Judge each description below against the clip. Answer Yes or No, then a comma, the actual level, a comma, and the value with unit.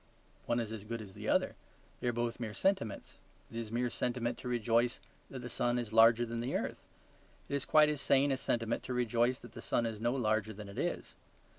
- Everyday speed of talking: No, fast, 230 wpm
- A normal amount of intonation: No, narrow, 1.6 semitones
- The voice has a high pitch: No, low, 120 Hz